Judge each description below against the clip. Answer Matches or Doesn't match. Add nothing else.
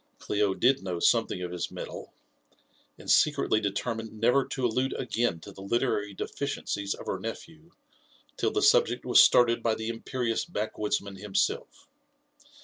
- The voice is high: Doesn't match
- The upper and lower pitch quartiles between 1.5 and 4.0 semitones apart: Doesn't match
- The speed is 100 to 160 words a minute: Matches